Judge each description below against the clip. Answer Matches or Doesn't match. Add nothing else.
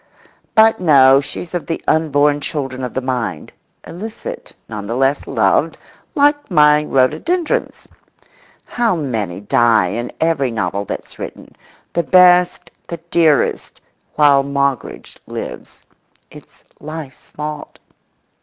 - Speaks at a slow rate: Matches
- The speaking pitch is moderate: Matches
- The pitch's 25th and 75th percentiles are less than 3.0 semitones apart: Doesn't match